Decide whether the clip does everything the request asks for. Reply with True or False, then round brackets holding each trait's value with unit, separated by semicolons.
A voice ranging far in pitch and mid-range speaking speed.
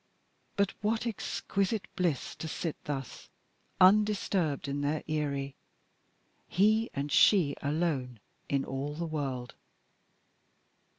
False (5.7 semitones; 105 wpm)